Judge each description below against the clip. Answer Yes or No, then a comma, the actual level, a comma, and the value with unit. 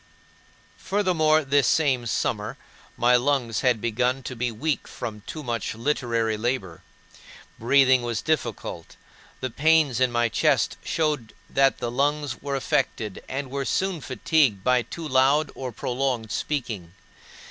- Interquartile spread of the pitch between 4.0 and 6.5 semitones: No, average, 3.6 semitones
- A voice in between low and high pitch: No, low, 130 Hz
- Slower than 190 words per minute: Yes, average, 140 wpm